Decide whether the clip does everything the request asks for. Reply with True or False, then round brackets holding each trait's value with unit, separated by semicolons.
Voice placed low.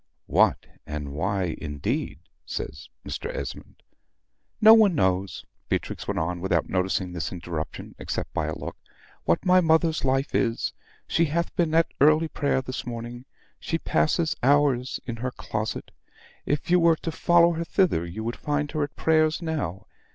True (130 Hz)